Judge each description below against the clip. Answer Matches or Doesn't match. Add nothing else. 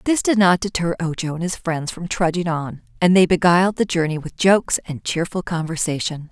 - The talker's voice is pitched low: Doesn't match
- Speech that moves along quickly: Matches